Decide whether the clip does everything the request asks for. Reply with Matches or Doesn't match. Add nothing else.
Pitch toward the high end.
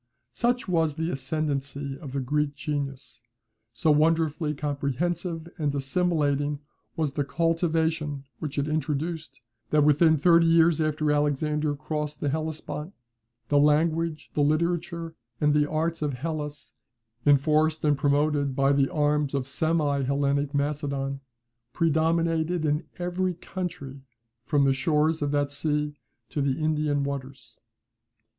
Doesn't match